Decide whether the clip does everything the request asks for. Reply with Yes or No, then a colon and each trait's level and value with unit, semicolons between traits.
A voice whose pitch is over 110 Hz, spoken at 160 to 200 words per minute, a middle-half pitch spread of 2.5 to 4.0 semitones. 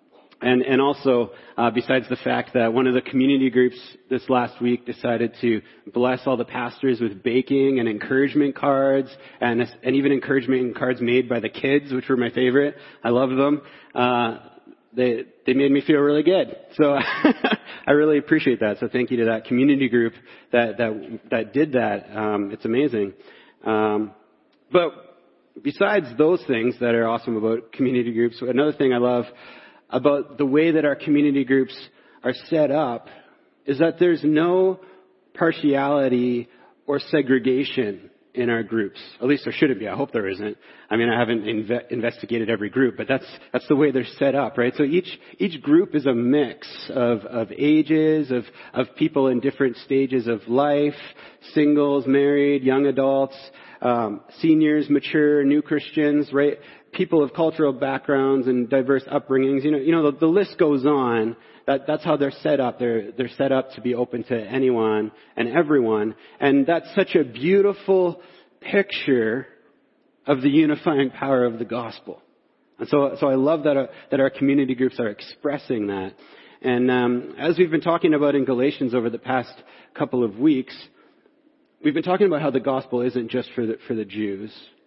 Yes: low, 135 Hz; average, 175 wpm; average, 3.2 semitones